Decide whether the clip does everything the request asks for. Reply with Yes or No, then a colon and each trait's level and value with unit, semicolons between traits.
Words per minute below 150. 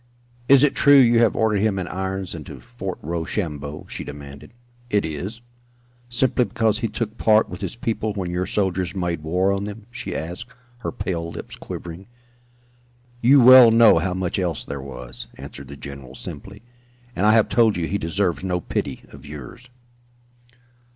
No: average, 175 wpm